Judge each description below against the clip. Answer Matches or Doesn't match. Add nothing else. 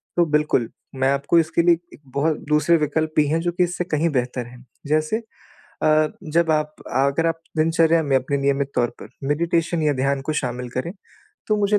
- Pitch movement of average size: Matches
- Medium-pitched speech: Matches